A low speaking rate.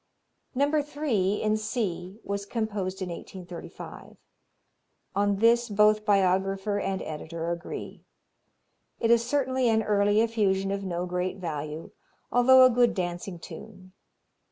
Yes: slow, 125 wpm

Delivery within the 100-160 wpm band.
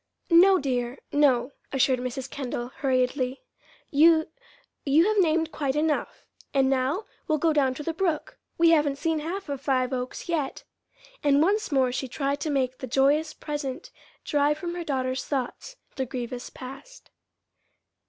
Yes: average, 155 wpm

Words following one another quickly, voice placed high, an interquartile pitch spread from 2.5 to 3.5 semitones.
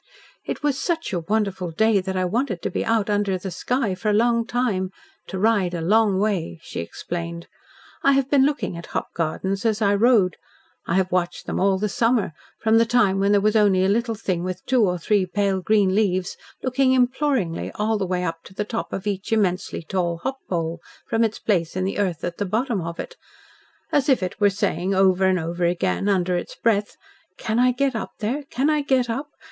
No: fast, 220 wpm; high, 200 Hz; average, 3.9 semitones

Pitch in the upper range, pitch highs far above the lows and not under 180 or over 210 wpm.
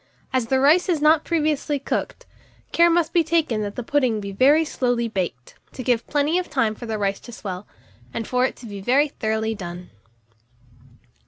Yes: very high, 250 Hz; wide, 5.8 semitones; average, 190 wpm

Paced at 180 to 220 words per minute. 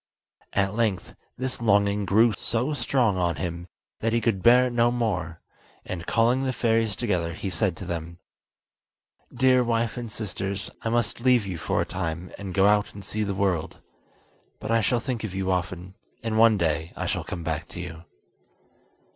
Yes: average, 185 wpm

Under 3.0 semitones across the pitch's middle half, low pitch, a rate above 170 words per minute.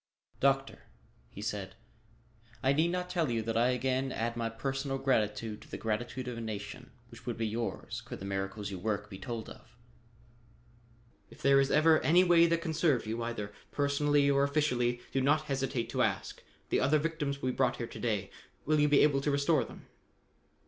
No: average, 3.9 semitones; low, 130 Hz; average, 195 wpm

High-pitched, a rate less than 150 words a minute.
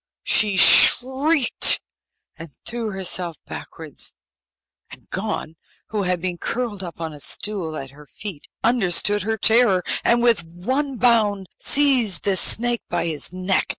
Yes: high, 200 Hz; average, 140 wpm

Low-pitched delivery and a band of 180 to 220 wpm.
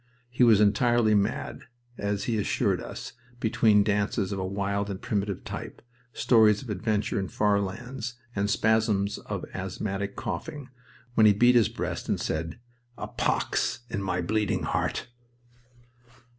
No: low, 105 Hz; average, 145 wpm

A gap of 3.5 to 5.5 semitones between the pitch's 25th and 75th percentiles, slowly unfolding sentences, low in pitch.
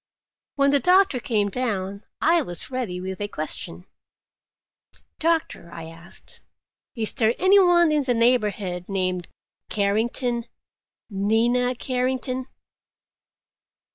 No: average, 5.2 semitones; slow, 110 wpm; high, 230 Hz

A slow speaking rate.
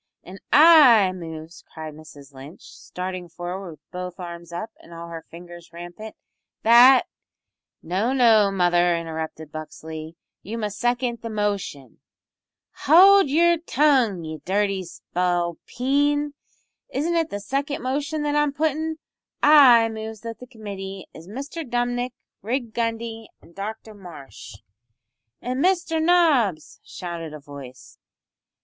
Yes: slow, 130 wpm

